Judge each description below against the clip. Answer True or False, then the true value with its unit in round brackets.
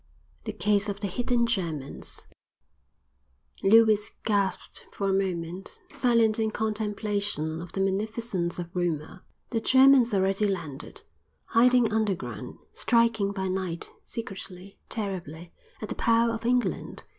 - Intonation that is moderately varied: True (3.6 semitones)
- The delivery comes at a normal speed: False (120 wpm)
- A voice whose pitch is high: True (200 Hz)